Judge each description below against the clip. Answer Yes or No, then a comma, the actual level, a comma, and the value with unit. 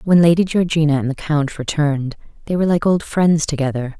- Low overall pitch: No, medium, 155 Hz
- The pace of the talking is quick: No, average, 195 wpm